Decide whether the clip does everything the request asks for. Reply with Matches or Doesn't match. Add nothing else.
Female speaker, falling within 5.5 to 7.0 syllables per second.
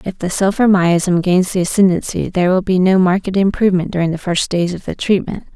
Matches